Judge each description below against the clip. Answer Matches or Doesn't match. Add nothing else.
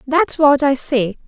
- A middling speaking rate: Matches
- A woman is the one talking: Matches